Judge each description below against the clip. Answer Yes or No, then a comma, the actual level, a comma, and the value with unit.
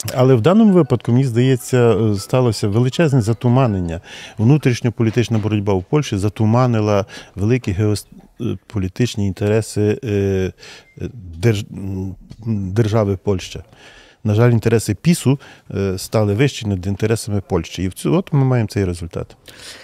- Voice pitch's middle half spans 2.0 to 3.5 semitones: No, average, 3.9 semitones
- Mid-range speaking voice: No, low, 110 Hz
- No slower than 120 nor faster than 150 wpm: No, slow, 105 wpm